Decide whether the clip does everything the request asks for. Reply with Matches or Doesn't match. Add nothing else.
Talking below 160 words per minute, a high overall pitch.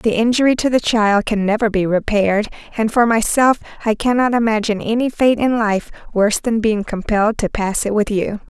Doesn't match